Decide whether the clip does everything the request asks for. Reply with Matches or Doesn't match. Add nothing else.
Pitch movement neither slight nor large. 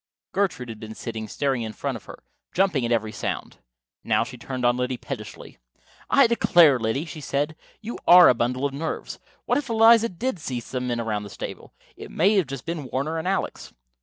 Doesn't match